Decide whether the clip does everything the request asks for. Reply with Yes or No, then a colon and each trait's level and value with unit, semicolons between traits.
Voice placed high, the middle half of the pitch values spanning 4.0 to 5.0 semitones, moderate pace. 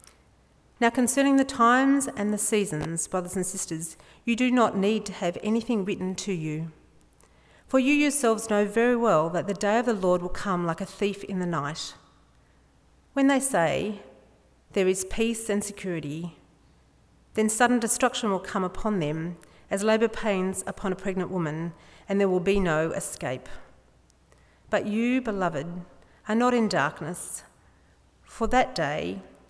Yes: high, 200 Hz; average, 4.5 semitones; average, 160 wpm